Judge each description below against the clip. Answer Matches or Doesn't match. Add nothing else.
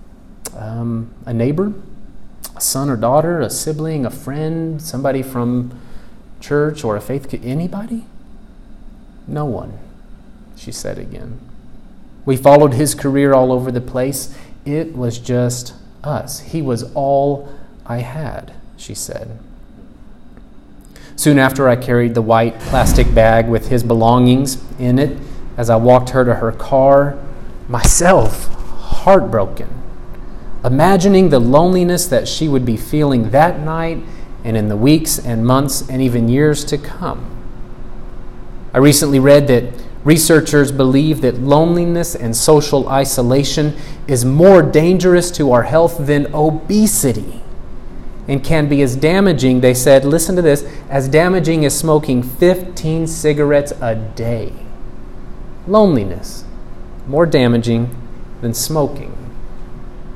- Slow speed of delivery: Matches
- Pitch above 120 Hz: Matches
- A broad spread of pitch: Doesn't match